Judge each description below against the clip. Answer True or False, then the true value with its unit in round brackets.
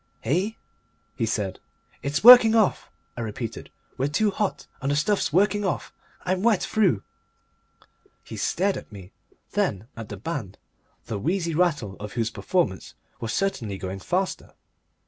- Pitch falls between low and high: True (150 Hz)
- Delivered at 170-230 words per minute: False (145 wpm)